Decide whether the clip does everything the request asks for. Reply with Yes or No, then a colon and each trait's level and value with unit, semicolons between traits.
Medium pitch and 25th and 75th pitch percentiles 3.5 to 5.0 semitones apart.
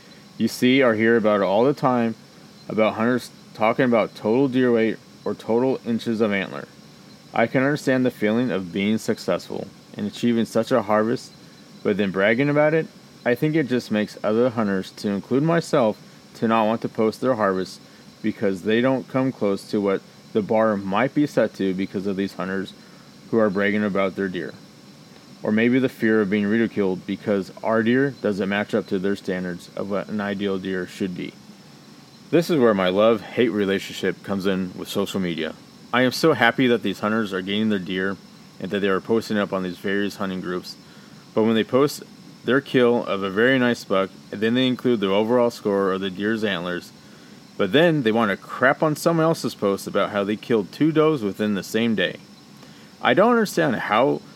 No: low, 110 Hz; average, 4.0 semitones